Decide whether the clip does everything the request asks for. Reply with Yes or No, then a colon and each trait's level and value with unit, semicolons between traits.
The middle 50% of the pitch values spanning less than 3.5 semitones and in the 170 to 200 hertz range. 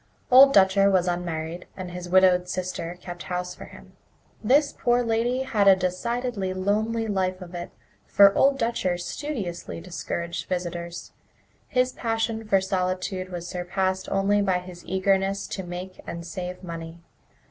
Yes: average, 2.8 semitones; medium, 185 Hz